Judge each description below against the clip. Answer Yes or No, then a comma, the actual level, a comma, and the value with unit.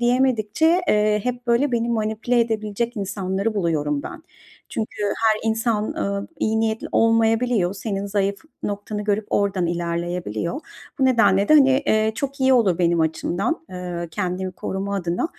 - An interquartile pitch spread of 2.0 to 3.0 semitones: No, average, 3.7 semitones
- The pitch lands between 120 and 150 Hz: No, high, 210 Hz